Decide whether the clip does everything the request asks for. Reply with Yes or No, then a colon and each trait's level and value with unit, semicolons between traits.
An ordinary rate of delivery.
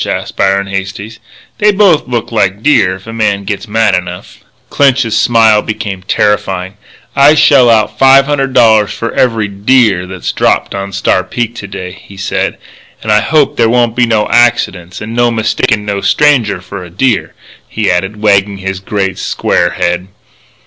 Yes: average, 170 wpm